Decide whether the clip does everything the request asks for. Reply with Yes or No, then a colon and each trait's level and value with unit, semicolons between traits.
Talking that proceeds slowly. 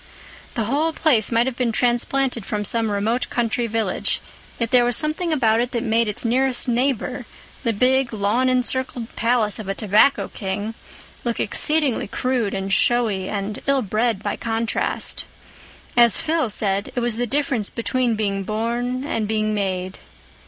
No: average, 160 wpm